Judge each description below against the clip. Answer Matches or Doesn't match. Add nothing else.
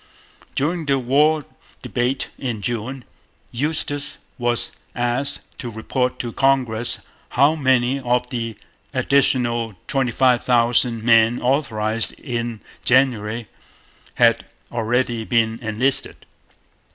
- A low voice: Matches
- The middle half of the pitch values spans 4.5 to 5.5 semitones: Doesn't match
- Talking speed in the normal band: Doesn't match